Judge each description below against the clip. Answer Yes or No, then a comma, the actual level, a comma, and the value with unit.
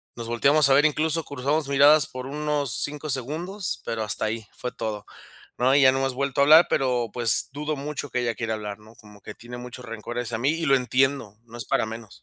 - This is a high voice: No, low, 130 Hz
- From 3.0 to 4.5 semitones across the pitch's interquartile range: Yes, average, 3.9 semitones